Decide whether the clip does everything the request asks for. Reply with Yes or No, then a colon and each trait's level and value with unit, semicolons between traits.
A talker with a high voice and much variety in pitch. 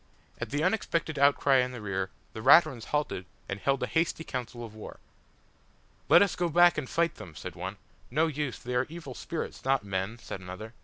No: low, 130 Hz; wide, 6.8 semitones